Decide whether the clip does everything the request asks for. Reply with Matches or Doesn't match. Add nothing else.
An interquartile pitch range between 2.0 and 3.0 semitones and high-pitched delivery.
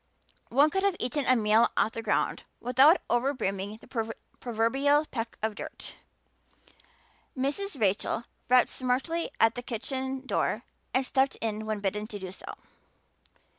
Doesn't match